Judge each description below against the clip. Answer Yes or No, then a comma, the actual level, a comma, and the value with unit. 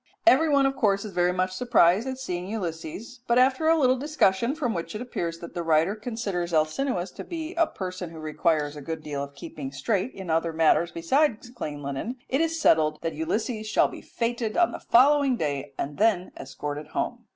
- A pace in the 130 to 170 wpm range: No, fast, 205 wpm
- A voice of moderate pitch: No, high, 195 Hz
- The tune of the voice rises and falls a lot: Yes, wide, 7.7 semitones